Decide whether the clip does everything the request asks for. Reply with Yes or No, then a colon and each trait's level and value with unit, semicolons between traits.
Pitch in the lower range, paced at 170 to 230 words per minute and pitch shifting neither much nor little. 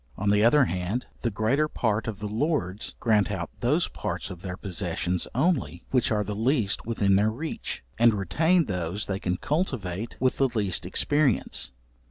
Yes: low, 105 Hz; average, 175 wpm; average, 5.0 semitones